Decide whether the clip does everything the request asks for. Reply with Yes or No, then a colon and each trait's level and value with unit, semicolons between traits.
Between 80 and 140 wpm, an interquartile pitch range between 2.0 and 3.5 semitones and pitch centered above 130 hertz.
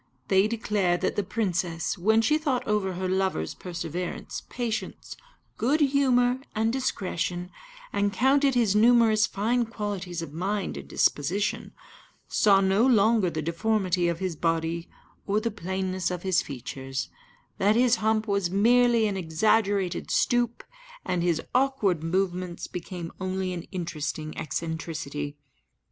No: slow, 135 wpm; average, 4.3 semitones; high, 190 Hz